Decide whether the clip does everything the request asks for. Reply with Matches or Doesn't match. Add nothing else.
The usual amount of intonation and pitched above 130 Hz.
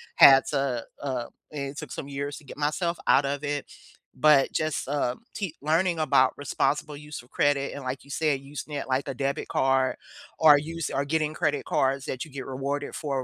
Doesn't match